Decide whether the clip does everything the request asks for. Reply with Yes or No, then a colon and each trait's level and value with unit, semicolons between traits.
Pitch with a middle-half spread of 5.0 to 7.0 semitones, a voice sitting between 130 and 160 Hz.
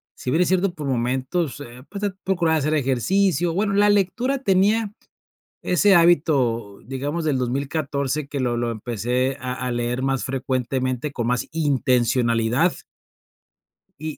Yes: wide, 5.6 semitones; medium, 140 Hz